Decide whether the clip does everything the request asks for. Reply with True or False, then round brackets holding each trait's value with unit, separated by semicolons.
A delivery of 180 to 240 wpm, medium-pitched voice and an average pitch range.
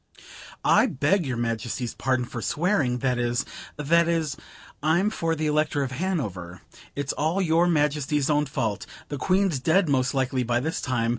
False (165 wpm; 145 Hz; 4.5 semitones)